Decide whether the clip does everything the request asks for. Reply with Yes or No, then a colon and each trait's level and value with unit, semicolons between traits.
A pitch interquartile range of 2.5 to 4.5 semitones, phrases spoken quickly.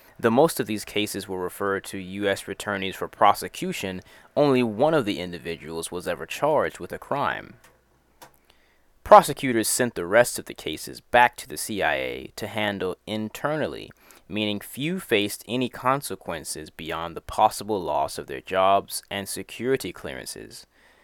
No: average, 3.9 semitones; average, 150 wpm